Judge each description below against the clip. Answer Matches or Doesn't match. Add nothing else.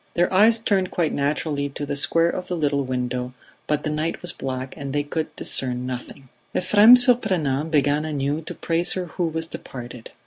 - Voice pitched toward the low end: Doesn't match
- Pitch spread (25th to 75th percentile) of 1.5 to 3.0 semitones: Doesn't match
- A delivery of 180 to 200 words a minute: Matches